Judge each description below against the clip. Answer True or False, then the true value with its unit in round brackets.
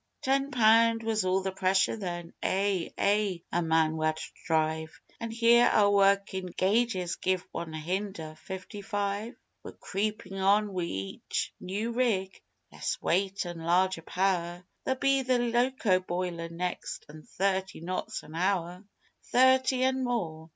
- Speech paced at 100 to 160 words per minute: True (145 wpm)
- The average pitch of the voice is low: False (190 Hz)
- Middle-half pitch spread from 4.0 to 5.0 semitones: True (4.3 semitones)